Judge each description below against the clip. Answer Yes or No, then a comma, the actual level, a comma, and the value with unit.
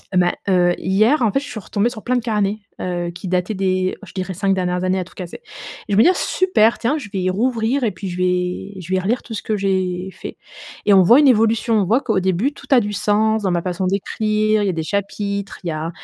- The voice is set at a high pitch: Yes, high, 200 Hz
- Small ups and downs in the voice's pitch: No, average, 3.2 semitones